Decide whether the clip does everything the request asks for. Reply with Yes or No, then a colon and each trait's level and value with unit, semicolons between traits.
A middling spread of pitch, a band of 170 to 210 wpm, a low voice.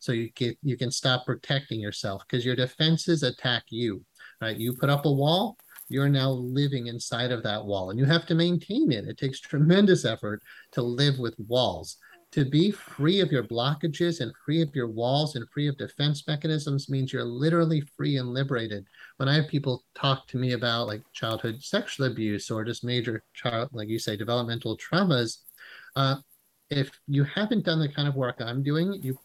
Yes: average, 3.9 semitones; average, 195 wpm; low, 130 Hz